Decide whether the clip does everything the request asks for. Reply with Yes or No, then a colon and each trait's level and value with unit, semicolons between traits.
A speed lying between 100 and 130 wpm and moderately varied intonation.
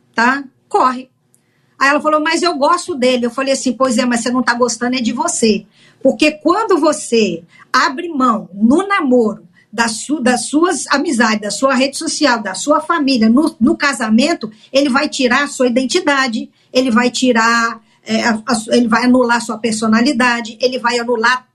No: average, 165 wpm; average, 3.5 semitones